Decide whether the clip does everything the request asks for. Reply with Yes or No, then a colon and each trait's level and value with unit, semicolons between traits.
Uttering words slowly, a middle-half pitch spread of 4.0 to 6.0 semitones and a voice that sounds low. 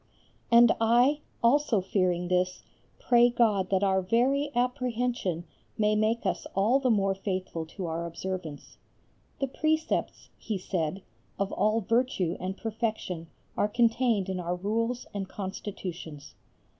No: slow, 130 wpm; average, 4.4 semitones; high, 205 Hz